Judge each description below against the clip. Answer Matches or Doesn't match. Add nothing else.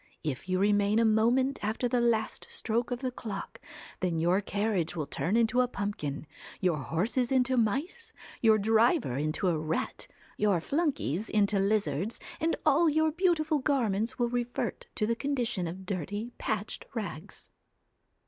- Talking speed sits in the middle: Matches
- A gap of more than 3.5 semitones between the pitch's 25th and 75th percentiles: Matches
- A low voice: Doesn't match